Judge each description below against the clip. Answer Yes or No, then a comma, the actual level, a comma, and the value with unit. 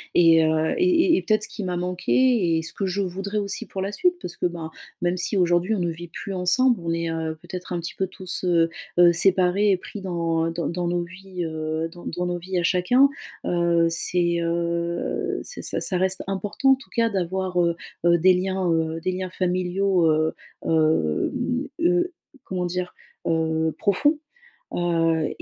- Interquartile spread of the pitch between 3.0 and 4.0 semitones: No, narrow, 2.4 semitones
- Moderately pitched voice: Yes, medium, 180 Hz